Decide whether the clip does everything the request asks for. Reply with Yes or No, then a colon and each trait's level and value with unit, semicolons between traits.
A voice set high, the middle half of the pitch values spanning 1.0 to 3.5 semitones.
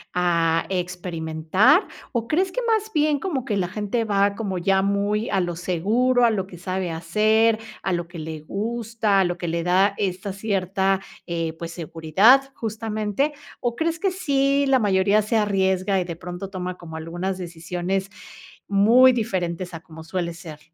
No: high, 195 Hz; average, 4.3 semitones